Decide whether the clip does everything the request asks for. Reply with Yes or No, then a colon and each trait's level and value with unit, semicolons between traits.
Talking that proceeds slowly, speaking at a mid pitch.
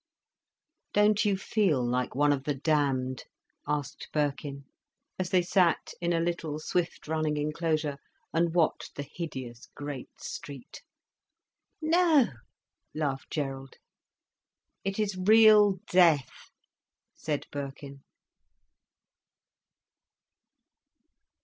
Yes: slow, 95 wpm; medium, 155 Hz